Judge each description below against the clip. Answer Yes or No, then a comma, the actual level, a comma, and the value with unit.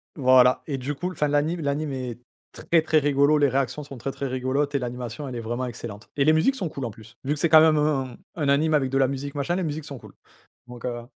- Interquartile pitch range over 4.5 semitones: No, average, 2.9 semitones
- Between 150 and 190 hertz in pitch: No, medium, 140 Hz